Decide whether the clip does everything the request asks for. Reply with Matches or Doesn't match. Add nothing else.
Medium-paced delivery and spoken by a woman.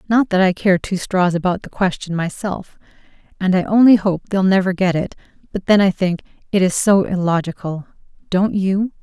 Matches